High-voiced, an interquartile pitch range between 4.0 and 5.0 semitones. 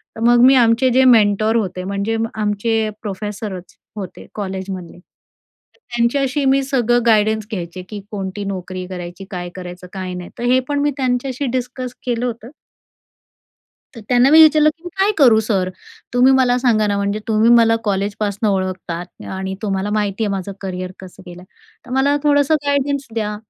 Yes: high, 215 Hz; average, 4.6 semitones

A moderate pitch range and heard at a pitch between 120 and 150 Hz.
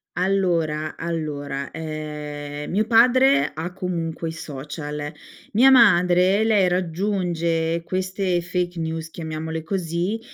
No: average, 3.1 semitones; medium, 170 Hz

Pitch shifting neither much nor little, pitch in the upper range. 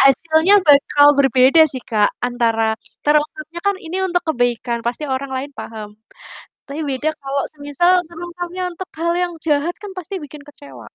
Yes: average, 4.5 semitones; very high, 290 Hz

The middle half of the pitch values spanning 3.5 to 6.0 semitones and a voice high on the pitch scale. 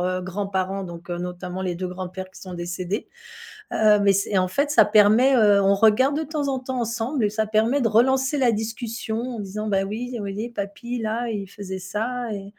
Yes: average, 3.9 semitones; high, 210 Hz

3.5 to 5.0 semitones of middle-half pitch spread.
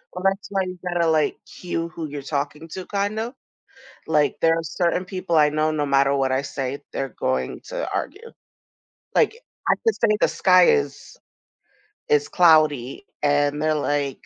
Yes: average, 4.4 semitones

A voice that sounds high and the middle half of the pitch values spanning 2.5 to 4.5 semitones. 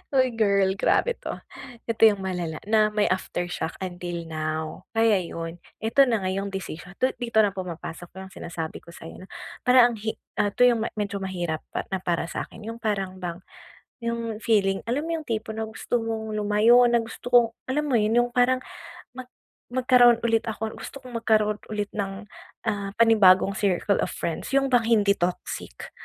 Yes: high, 215 Hz; average, 3.8 semitones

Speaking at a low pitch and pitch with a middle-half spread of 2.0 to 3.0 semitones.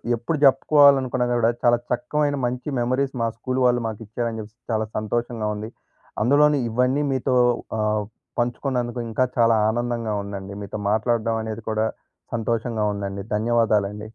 Yes: low, 115 Hz; narrow, 2.6 semitones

